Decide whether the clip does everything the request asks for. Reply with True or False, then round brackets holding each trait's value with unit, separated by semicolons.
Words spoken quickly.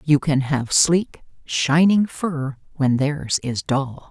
False (145 wpm)